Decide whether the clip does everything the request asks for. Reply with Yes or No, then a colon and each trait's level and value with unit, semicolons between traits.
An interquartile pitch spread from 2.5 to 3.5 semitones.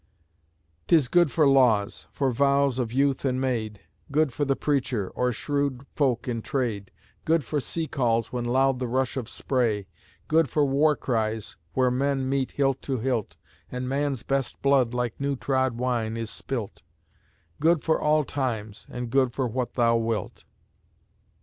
Yes: average, 3.0 semitones